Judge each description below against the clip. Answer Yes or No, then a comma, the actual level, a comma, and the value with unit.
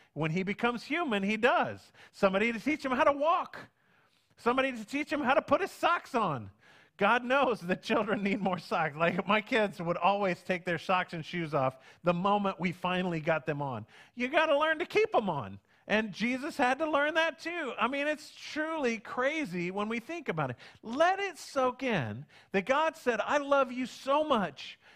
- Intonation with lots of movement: Yes, wide, 7.9 semitones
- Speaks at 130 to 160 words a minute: No, fast, 205 wpm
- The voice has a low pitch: No, high, 230 Hz